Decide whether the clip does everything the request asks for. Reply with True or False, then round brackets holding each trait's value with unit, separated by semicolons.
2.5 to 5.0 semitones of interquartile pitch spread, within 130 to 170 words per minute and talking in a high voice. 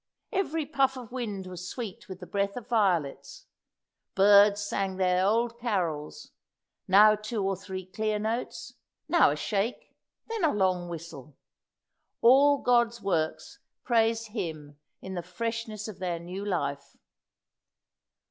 True (4.2 semitones; 135 wpm; 205 Hz)